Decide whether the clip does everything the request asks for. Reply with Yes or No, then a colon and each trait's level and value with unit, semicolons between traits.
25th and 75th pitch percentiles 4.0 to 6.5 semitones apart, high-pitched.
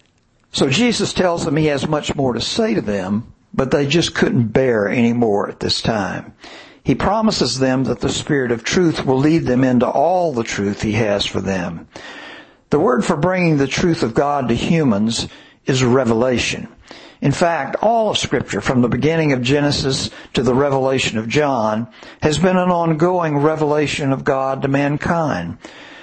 No: wide, 5.4 semitones; medium, 140 Hz